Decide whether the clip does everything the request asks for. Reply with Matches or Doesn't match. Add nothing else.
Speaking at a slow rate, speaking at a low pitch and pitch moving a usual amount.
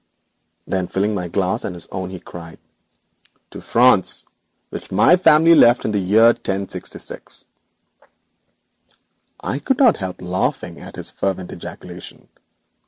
Matches